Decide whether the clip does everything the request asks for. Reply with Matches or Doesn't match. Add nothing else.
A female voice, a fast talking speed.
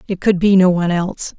Matches